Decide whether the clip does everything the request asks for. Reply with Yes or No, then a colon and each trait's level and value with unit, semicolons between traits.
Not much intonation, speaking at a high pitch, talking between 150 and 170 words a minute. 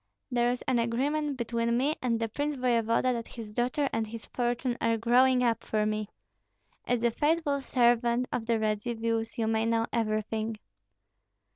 Yes: narrow, 1.8 semitones; high, 235 Hz; average, 165 wpm